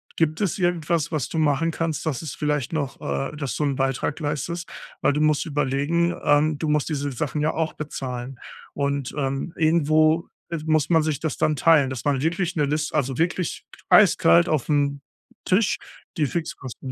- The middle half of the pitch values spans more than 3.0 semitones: No, narrow, 2.5 semitones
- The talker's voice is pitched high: No, medium, 150 Hz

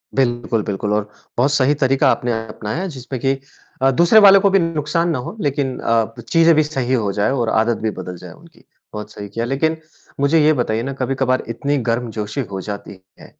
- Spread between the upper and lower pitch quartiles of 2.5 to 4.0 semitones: No, average, 5.2 semitones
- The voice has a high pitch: No, low, 130 Hz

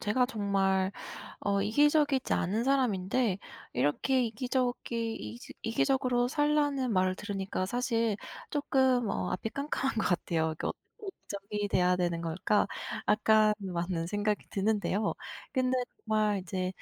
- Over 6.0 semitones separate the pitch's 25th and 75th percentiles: No, average, 5.1 semitones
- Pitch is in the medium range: No, high, 210 Hz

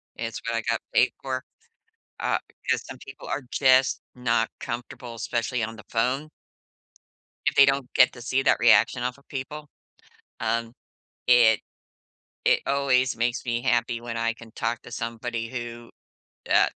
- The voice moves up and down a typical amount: No, narrow, 2.1 semitones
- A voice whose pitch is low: Yes, low, 120 Hz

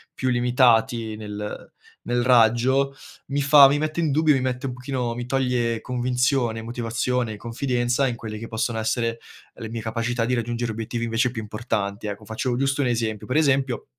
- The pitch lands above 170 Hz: No, low, 120 Hz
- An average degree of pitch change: No, narrow, 2.2 semitones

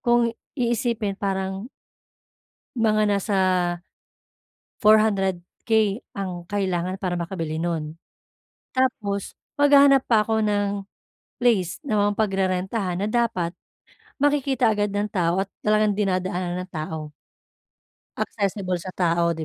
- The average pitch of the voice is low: No, high, 200 Hz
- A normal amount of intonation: Yes, average, 3.3 semitones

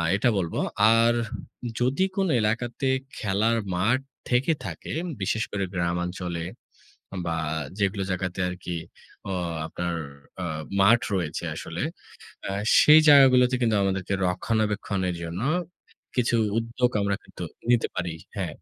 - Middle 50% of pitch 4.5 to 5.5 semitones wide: Yes, average, 5.0 semitones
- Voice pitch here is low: Yes, low, 100 Hz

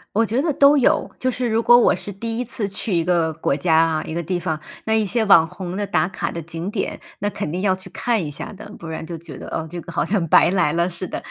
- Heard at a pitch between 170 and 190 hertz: Yes, medium, 185 Hz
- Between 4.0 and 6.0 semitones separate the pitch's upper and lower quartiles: Yes, average, 4.8 semitones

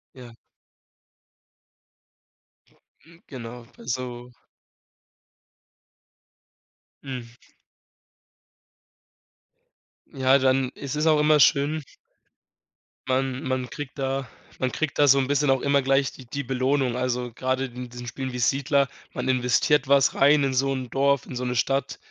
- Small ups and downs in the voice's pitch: Yes, narrow, 1.8 semitones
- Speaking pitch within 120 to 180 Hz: Yes, low, 130 Hz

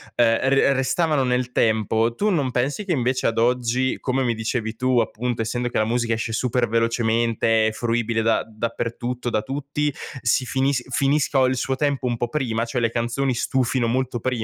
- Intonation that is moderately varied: No, narrow, 2.3 semitones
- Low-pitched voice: Yes, low, 120 Hz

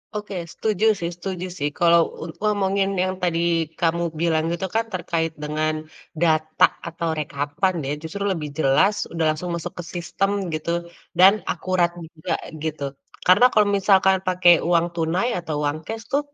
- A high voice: No, medium, 170 Hz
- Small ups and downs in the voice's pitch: No, average, 3.0 semitones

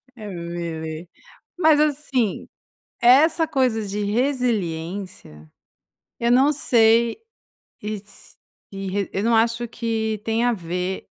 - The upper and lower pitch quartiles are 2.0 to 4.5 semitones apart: No, average, 4.9 semitones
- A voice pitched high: Yes, high, 225 Hz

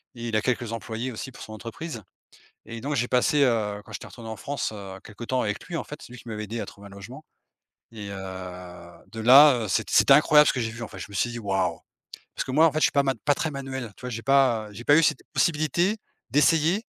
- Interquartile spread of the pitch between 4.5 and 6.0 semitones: Yes, average, 4.9 semitones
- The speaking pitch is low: Yes, low, 120 Hz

